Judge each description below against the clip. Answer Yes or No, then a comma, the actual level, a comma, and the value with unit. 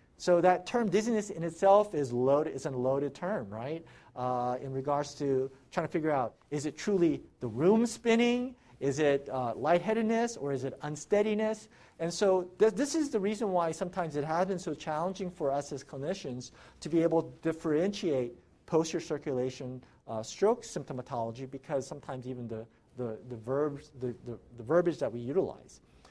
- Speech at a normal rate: Yes, average, 175 wpm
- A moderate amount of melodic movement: No, wide, 6.1 semitones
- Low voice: No, medium, 150 Hz